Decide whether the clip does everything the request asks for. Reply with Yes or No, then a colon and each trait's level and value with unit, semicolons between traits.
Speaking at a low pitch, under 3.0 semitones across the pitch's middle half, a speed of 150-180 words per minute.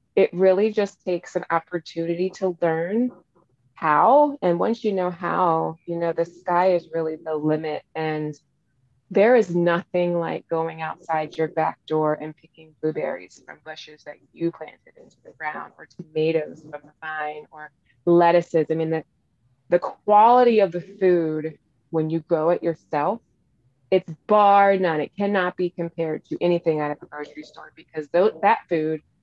No: medium, 165 Hz; narrow, 2.4 semitones; average, 165 wpm